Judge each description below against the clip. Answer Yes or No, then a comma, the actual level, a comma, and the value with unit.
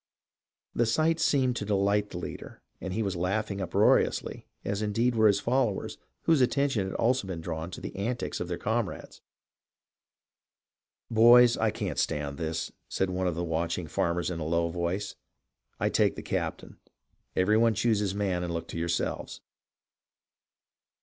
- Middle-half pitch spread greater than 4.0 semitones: Yes, average, 4.6 semitones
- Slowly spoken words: No, average, 170 wpm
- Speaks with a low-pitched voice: Yes, low, 100 Hz